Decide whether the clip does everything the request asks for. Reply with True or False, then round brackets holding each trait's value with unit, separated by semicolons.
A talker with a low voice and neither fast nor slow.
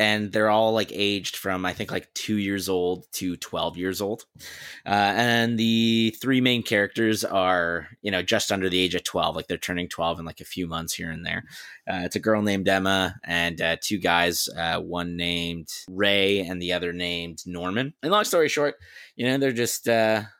False (100 Hz; 210 wpm)